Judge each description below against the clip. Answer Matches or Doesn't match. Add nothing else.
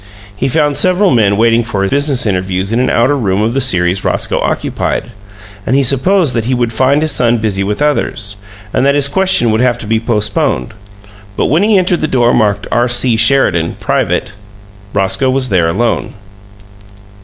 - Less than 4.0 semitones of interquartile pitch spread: Doesn't match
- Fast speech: Doesn't match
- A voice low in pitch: Matches